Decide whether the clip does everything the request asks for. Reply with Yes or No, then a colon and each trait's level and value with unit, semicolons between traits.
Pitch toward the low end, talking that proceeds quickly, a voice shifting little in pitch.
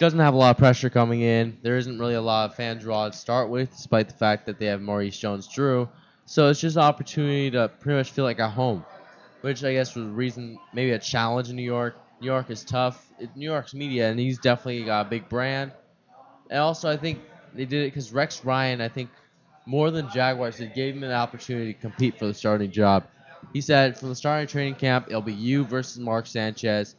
No: low, 125 Hz; fast, 235 wpm; average, 3.2 semitones